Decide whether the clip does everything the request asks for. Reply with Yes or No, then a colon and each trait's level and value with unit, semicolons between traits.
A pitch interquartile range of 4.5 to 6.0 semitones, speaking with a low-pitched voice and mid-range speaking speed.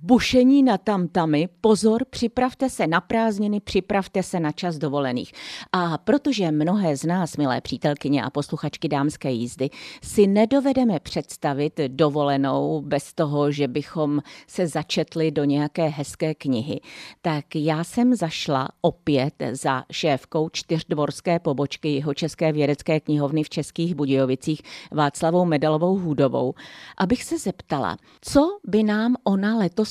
No: average, 5.2 semitones; medium, 160 Hz; average, 130 wpm